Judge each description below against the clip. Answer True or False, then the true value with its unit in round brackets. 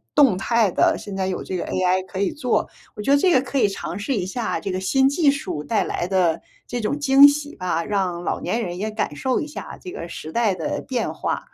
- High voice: True (210 Hz)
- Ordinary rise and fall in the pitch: False (6.5 semitones)